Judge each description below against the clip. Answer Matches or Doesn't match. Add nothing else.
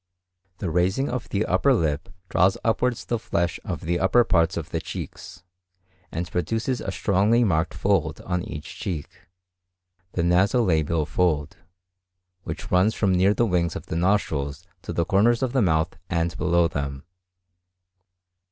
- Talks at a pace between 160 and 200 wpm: Doesn't match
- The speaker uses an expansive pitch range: Doesn't match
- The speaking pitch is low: Matches